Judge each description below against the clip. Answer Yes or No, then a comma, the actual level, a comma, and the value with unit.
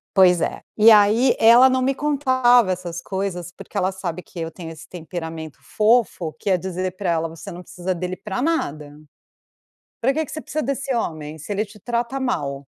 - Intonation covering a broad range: Yes, wide, 6.3 semitones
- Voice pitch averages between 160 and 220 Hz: Yes, high, 190 Hz